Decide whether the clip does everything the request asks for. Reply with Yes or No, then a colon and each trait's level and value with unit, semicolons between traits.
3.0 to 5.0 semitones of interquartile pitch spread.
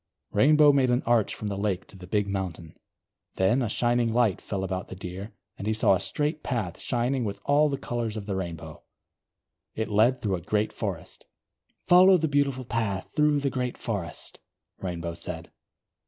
No: wide, 5.4 semitones